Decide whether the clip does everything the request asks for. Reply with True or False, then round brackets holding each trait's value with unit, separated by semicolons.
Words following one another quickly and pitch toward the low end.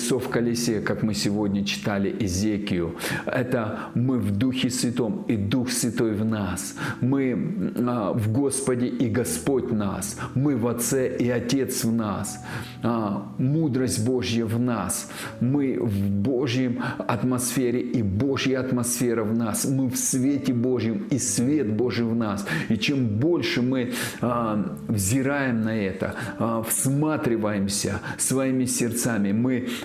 False (125 wpm; 120 Hz)